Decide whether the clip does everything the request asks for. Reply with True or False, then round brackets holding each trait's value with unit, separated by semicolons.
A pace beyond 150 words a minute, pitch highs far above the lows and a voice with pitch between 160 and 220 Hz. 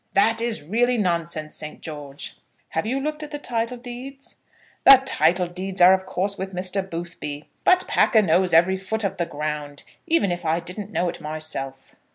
True (185 wpm; 5.8 semitones; 185 Hz)